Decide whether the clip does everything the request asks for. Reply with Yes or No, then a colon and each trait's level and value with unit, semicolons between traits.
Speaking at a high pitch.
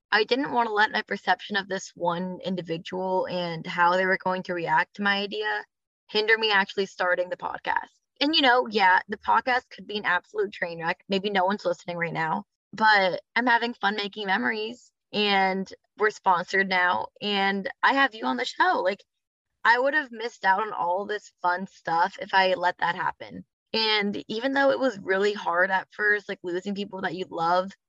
Yes: high, 195 Hz